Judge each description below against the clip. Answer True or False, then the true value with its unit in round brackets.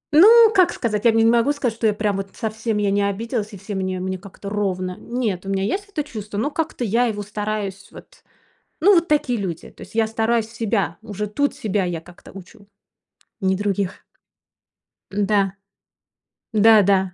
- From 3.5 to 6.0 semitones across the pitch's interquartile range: False (3.0 semitones)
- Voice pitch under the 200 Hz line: False (210 Hz)